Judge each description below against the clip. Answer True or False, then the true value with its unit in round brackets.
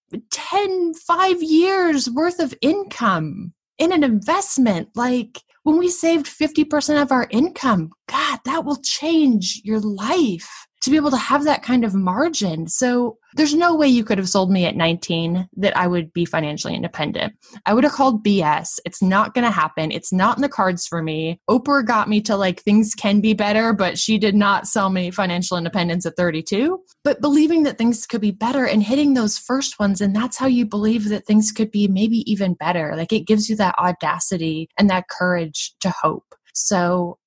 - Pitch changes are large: True (7.2 semitones)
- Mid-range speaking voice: False (215 Hz)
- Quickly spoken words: False (195 wpm)